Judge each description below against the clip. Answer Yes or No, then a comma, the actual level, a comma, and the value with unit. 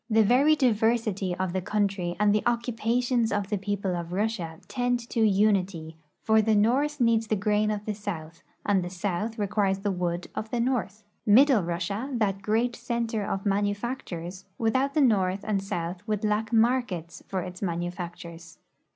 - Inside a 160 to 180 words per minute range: Yes, average, 170 wpm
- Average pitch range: Yes, average, 3.7 semitones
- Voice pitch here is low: No, high, 205 Hz